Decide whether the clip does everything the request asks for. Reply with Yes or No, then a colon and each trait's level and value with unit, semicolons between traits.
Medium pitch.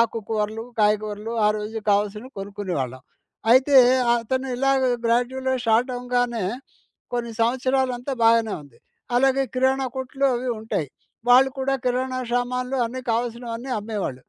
No: high, 240 Hz